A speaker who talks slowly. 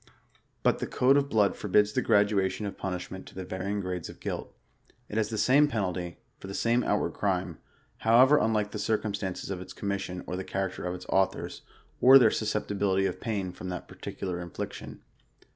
No: average, 195 wpm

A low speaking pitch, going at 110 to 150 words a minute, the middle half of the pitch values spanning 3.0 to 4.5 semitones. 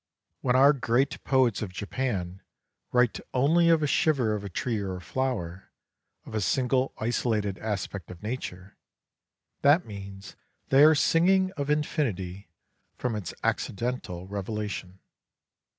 No: low, 115 Hz; slow, 135 wpm; wide, 5.5 semitones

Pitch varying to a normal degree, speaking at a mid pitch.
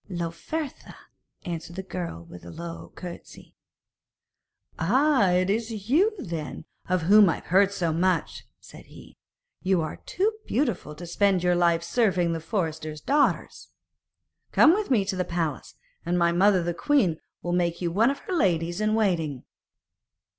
Yes: average, 4.1 semitones; medium, 180 Hz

